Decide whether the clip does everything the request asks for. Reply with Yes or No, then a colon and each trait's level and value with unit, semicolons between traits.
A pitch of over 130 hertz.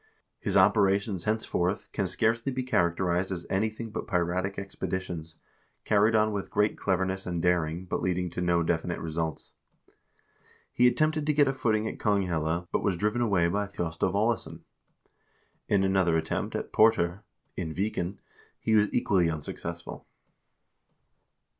No: very low, 95 Hz